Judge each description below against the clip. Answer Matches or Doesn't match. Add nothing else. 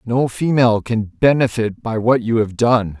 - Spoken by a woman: Doesn't match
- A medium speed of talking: Matches